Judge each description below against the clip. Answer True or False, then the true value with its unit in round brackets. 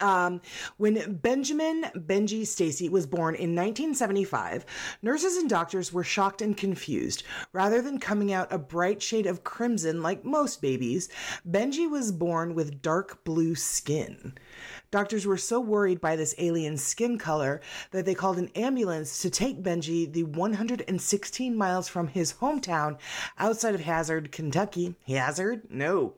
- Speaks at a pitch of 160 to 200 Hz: True (190 Hz)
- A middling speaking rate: True (145 wpm)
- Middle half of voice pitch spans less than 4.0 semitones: False (4.7 semitones)